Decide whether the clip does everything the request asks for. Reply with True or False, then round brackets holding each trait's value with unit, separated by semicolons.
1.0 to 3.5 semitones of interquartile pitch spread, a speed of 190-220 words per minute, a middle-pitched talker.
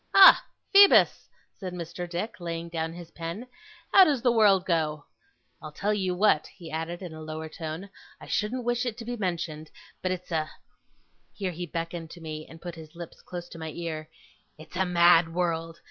True (2.7 semitones; 195 wpm; 170 Hz)